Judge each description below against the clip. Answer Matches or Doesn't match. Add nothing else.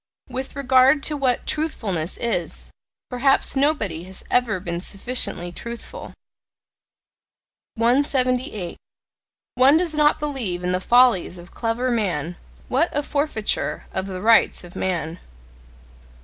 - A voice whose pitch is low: Doesn't match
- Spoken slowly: Matches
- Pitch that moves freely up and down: Matches